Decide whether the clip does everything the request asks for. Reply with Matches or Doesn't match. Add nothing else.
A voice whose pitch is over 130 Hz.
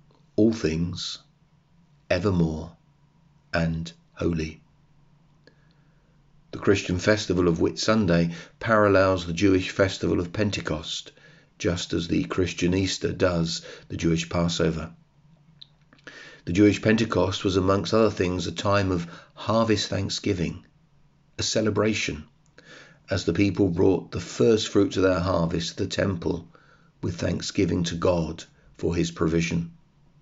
Doesn't match